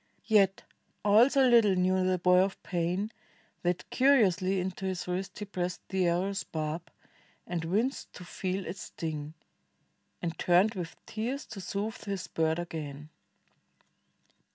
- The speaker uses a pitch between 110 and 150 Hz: No, medium, 185 Hz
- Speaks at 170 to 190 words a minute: No, average, 150 wpm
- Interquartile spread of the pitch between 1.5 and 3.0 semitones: Yes, average, 2.7 semitones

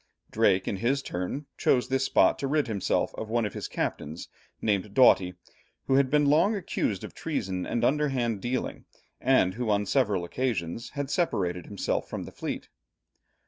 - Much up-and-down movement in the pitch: Yes, wide, 5.8 semitones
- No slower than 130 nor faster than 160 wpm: No, average, 170 wpm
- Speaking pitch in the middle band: No, low, 115 Hz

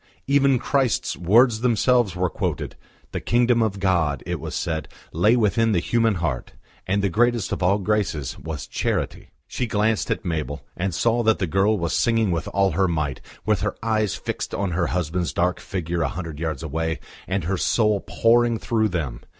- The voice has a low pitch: Yes, very low, 95 Hz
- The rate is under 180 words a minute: No, average, 185 wpm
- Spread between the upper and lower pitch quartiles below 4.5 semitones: No, average, 5.2 semitones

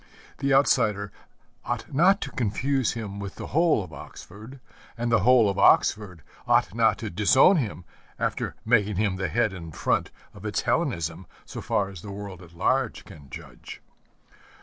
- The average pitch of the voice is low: Yes, low, 105 Hz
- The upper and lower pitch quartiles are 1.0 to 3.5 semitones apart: No, average, 5.2 semitones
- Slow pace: No, average, 170 wpm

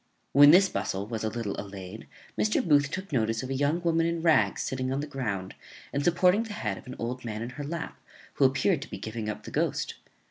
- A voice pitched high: No, low, 135 Hz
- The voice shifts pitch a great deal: Yes, wide, 6.7 semitones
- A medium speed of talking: No, fast, 235 wpm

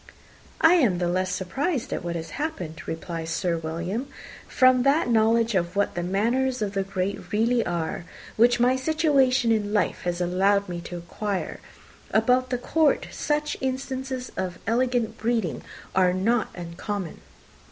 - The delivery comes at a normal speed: Yes, average, 150 wpm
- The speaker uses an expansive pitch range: Yes, wide, 6.0 semitones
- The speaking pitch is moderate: No, high, 215 Hz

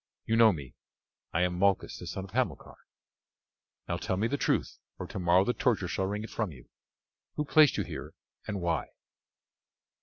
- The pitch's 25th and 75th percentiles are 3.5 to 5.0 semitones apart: Yes, average, 4.4 semitones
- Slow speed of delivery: No, average, 180 wpm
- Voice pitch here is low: Yes, low, 100 Hz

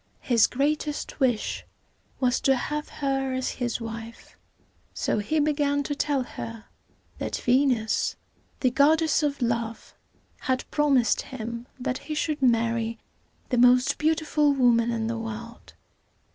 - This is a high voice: Yes, very high, 255 Hz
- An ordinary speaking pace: No, slow, 130 wpm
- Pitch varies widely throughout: No, average, 3.7 semitones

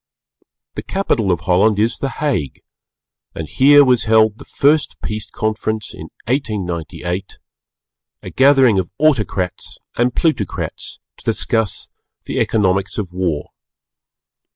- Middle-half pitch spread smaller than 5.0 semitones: No, wide, 5.6 semitones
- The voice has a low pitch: Yes, low, 110 Hz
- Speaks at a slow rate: Yes, slow, 120 wpm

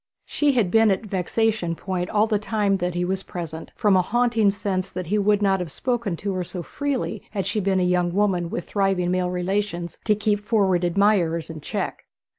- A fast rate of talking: Yes, fast, 210 wpm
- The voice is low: No, high, 195 Hz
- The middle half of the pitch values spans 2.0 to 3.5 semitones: Yes, average, 2.8 semitones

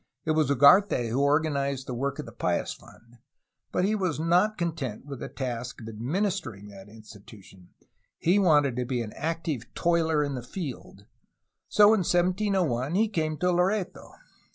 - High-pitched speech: No, medium, 145 Hz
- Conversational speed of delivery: Yes, average, 170 wpm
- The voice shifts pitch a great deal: Yes, wide, 6.6 semitones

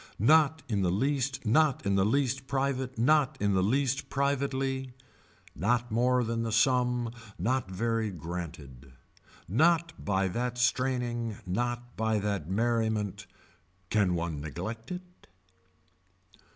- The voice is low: Yes, low, 120 Hz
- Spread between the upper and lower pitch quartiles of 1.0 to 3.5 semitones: No, average, 4.8 semitones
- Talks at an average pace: No, slow, 125 wpm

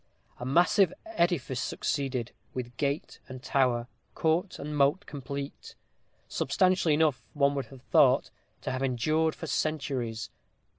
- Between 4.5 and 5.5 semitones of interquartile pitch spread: No, average, 3.6 semitones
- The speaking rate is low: Yes, slow, 130 wpm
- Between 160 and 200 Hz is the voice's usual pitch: No, medium, 140 Hz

